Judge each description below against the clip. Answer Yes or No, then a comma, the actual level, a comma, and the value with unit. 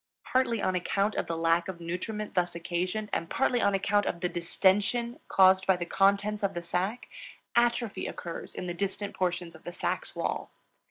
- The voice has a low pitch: No, high, 190 Hz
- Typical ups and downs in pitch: Yes, average, 3.2 semitones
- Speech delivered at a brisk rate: No, average, 185 wpm